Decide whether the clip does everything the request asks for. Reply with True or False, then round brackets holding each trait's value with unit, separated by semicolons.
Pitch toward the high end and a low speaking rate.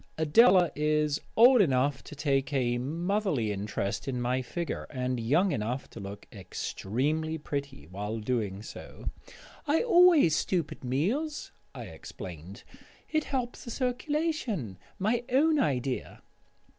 False (145 Hz; 130 wpm)